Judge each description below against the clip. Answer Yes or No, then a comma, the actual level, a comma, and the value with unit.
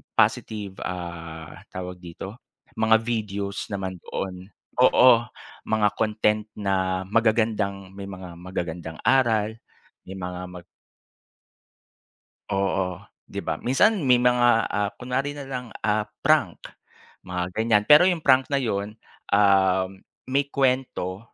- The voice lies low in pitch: Yes, low, 105 Hz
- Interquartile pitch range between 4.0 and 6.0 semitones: Yes, average, 4.5 semitones